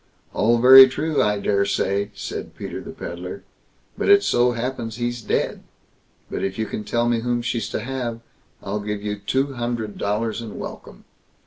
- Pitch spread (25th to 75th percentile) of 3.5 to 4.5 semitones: No, average, 2.9 semitones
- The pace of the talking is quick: No, average, 175 wpm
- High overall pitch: No, low, 115 Hz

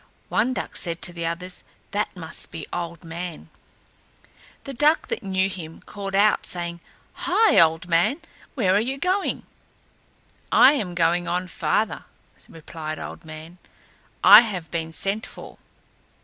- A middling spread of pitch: Yes, average, 4.0 semitones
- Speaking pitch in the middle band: Yes, medium, 180 Hz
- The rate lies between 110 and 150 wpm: Yes, average, 145 wpm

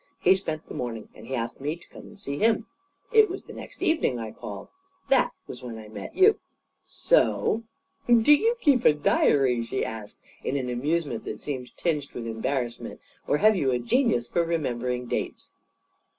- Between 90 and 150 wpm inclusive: No, average, 190 wpm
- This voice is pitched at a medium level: Yes, medium, 145 Hz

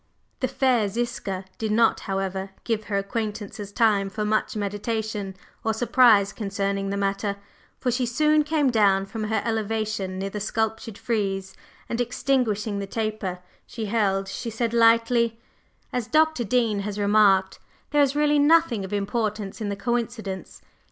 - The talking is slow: No, average, 150 wpm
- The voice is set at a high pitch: Yes, high, 215 Hz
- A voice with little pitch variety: No, average, 3.0 semitones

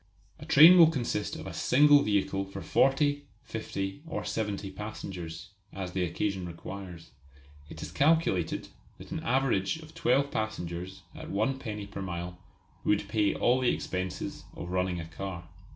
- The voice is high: No, low, 100 Hz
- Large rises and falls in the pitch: Yes, wide, 6.0 semitones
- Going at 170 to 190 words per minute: No, average, 155 wpm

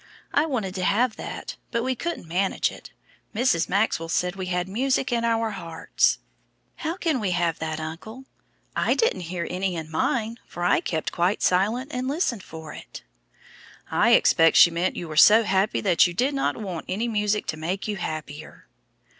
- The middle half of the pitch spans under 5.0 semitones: No, wide, 5.4 semitones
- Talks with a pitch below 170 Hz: No, high, 195 Hz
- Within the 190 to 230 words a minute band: No, average, 180 wpm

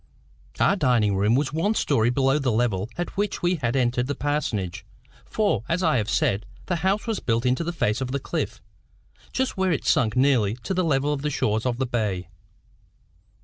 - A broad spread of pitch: Yes, wide, 6.4 semitones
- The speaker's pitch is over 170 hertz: No, low, 130 Hz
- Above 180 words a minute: Yes, average, 200 wpm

